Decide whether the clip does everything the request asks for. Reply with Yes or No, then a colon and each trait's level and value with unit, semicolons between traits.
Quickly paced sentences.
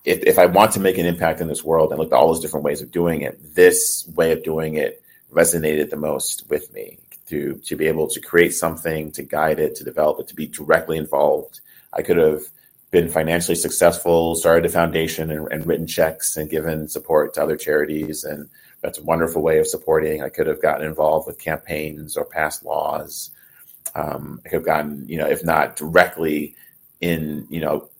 Yes: fast, 210 wpm